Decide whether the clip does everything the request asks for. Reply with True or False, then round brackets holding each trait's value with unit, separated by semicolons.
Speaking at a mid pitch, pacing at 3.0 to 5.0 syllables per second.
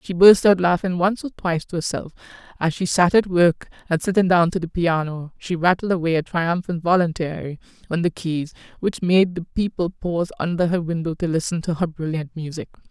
False (170 Hz; 5.5 syllables/s)